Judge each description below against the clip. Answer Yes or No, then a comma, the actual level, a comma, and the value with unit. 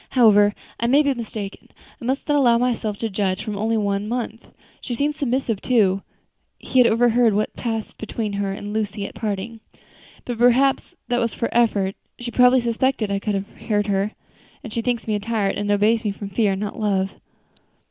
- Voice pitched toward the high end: Yes, high, 220 Hz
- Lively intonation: No, average, 2.8 semitones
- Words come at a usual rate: Yes, average, 190 wpm